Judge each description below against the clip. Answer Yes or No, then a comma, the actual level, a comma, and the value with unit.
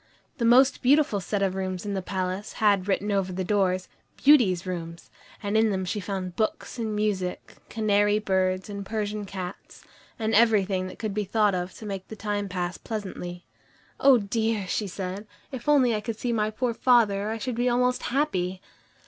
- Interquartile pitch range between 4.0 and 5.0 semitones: No, average, 3.0 semitones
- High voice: Yes, high, 205 Hz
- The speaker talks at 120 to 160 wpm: No, average, 185 wpm